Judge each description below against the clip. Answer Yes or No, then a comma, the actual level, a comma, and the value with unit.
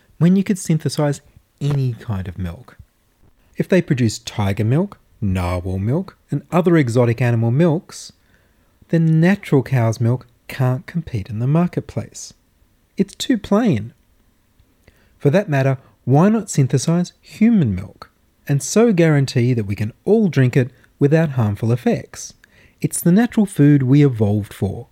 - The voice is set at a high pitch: No, low, 130 Hz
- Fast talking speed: No, average, 140 wpm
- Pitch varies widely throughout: Yes, wide, 7.4 semitones